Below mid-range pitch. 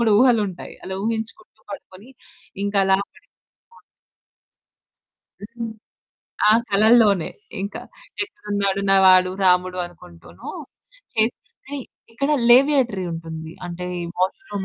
No: high, 200 Hz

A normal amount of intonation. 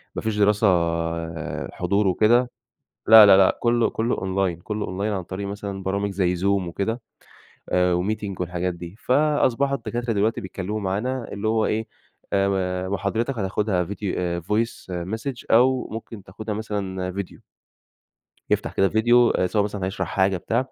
Yes: average, 3.0 semitones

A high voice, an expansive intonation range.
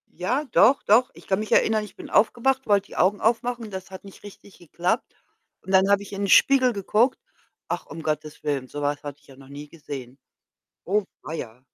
Yes: high, 195 Hz; wide, 6.6 semitones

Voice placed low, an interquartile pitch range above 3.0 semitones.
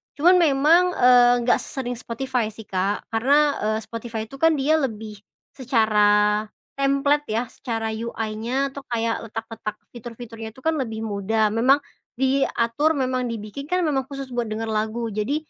No: high, 235 Hz; average, 3.8 semitones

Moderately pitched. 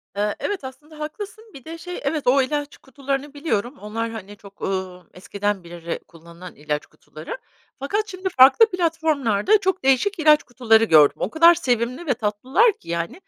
No: very high, 260 Hz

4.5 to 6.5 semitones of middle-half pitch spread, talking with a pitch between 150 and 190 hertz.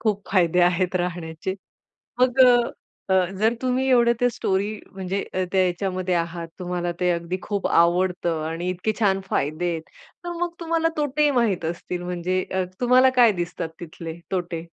No: average, 4.0 semitones; medium, 185 Hz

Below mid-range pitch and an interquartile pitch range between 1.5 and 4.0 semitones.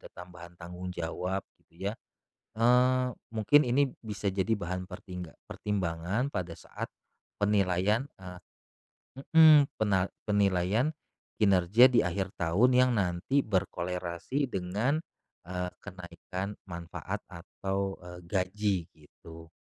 Yes: very low, 95 Hz; average, 3.6 semitones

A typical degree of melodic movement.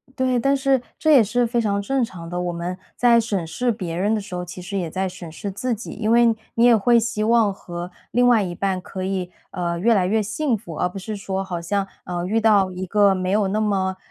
Yes: average, 4.1 semitones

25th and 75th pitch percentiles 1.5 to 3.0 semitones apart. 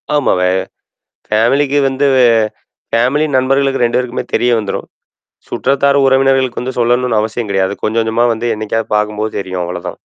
No: average, 3.7 semitones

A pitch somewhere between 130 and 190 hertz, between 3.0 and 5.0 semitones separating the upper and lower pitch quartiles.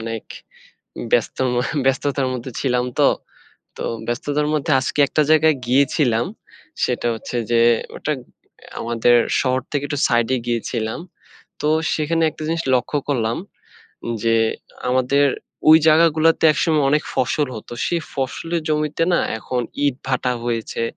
Yes: low, 135 Hz; average, 4.0 semitones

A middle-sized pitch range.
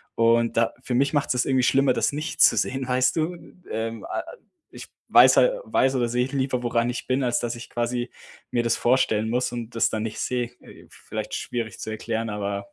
No: narrow, 2.1 semitones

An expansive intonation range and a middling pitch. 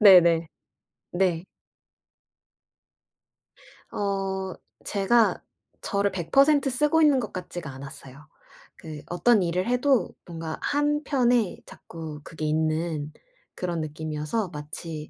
Yes: wide, 6.5 semitones; medium, 180 Hz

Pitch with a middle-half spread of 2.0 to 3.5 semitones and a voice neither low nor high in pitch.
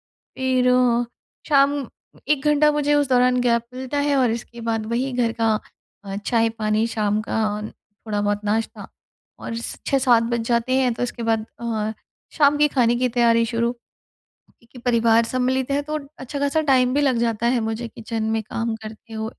No: narrow, 2.6 semitones; high, 235 Hz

